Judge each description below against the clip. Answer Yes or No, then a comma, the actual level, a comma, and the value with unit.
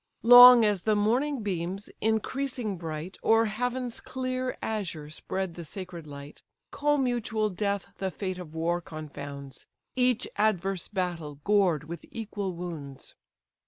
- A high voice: Yes, high, 195 Hz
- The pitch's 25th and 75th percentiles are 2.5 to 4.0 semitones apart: No, average, 5.0 semitones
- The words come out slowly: Yes, slow, 125 wpm